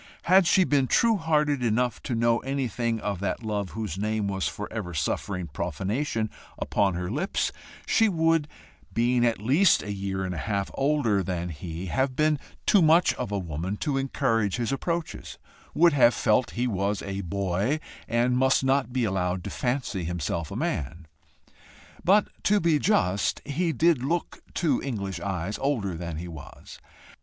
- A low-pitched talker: Yes, low, 115 Hz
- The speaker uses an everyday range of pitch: No, wide, 6.6 semitones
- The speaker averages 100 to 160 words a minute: No, average, 170 wpm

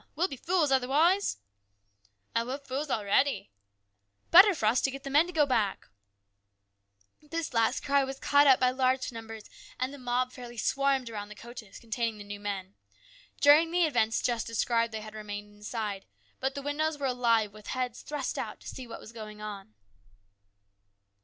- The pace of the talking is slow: No, average, 190 wpm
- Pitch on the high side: Yes, high, 240 Hz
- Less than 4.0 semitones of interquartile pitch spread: No, average, 4.8 semitones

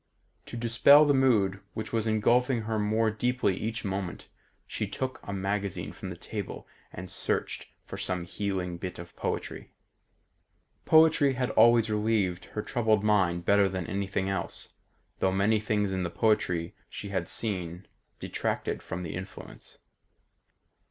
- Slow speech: No, average, 145 wpm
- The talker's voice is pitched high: No, low, 100 Hz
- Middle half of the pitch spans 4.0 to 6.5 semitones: No, average, 3.3 semitones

